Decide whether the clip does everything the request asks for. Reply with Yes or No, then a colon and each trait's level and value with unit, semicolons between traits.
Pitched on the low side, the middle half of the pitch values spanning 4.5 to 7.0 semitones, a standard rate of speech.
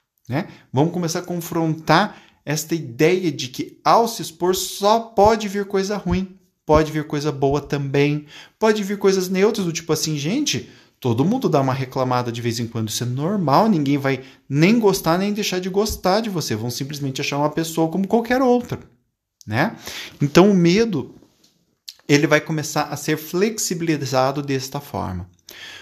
No: medium, 160 Hz; average, 5.1 semitones; average, 165 wpm